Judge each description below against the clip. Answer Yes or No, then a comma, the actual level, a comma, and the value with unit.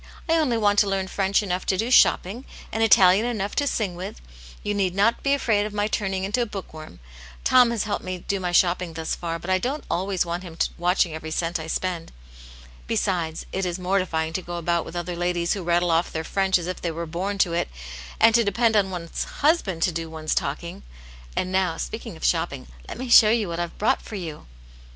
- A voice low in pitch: No, medium, 185 Hz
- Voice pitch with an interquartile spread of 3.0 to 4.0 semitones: Yes, average, 3.3 semitones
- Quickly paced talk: Yes, fast, 230 wpm